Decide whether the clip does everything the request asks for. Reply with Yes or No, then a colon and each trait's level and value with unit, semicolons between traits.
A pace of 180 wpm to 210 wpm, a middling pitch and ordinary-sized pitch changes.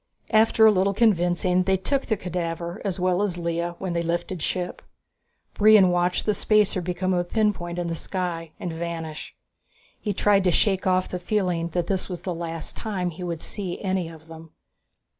No: average, 185 wpm; medium, 180 Hz; narrow, 2.3 semitones